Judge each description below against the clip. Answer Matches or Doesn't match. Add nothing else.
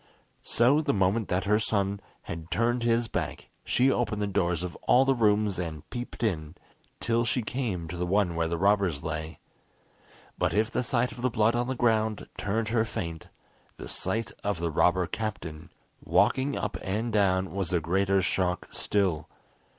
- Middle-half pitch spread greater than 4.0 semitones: Matches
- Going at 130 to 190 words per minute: Matches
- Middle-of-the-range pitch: Doesn't match